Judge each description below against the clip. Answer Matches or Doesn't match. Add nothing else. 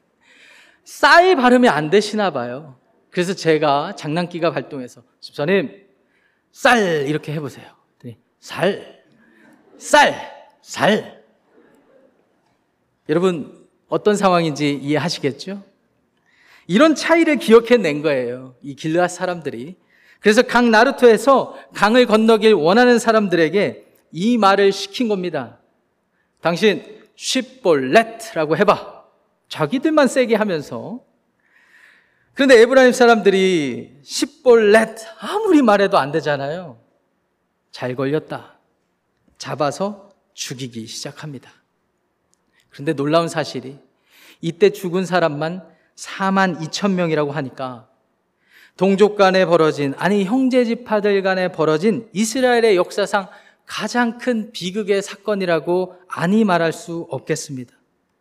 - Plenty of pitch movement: Matches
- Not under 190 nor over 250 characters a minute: Matches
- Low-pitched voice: Doesn't match